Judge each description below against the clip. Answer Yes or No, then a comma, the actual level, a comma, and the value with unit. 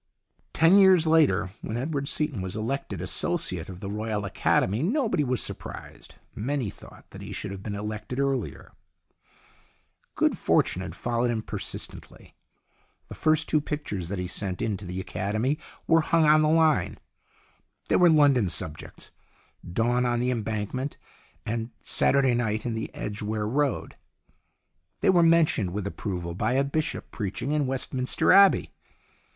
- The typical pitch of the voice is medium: No, low, 120 Hz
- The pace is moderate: Yes, average, 160 wpm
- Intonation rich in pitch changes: Yes, wide, 6.3 semitones